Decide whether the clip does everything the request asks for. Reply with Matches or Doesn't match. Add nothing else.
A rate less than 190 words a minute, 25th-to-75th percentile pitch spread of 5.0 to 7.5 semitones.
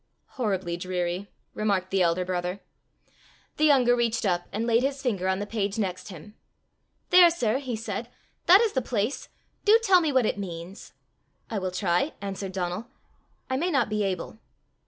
Matches